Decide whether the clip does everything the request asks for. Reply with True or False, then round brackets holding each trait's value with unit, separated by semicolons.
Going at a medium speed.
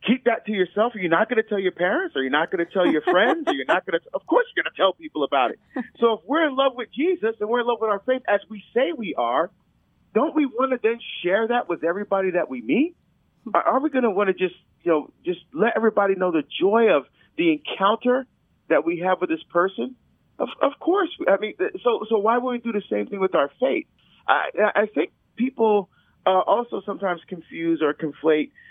False (245 wpm)